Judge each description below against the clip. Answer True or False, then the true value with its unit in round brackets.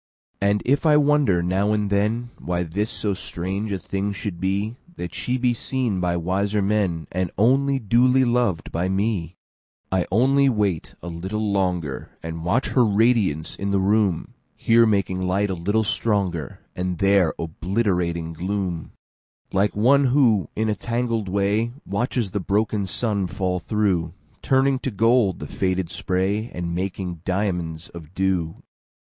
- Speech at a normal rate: False (130 wpm)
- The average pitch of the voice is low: True (100 Hz)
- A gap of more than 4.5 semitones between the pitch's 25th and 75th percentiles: False (3.8 semitones)